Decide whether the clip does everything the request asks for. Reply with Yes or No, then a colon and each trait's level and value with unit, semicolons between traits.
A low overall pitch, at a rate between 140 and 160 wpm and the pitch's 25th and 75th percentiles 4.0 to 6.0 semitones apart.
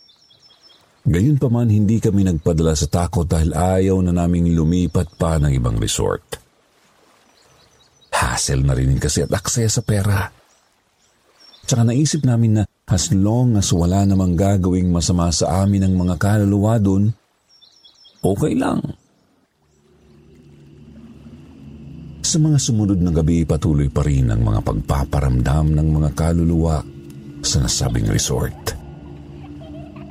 No: very low, 85 Hz; average, 120 wpm; wide, 5.4 semitones